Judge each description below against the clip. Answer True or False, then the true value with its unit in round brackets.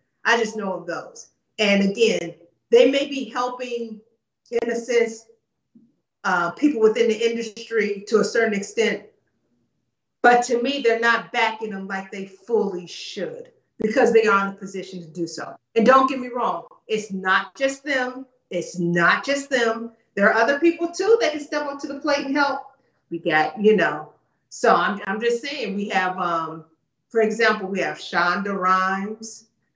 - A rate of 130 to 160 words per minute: False (175 wpm)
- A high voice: True (225 Hz)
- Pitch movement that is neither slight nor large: True (4.3 semitones)